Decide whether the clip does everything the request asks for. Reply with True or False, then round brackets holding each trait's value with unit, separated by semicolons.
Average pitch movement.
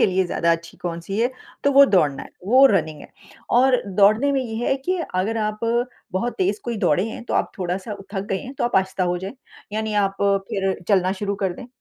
True (4.6 semitones)